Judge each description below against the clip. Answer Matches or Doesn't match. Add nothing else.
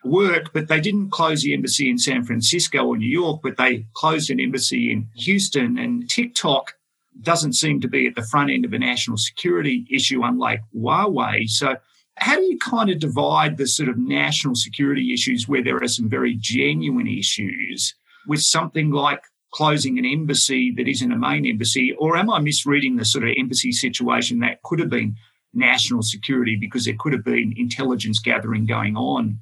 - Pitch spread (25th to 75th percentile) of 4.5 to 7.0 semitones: Matches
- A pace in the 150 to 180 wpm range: Doesn't match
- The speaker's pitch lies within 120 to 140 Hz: Matches